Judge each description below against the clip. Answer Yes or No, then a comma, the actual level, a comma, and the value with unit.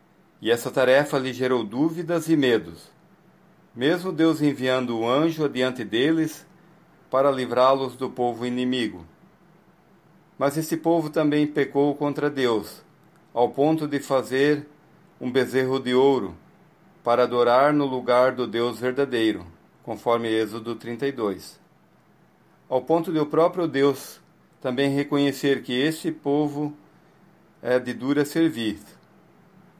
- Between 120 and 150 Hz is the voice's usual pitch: Yes, medium, 140 Hz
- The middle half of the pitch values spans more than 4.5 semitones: No, average, 3.9 semitones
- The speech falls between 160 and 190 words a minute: No, average, 125 wpm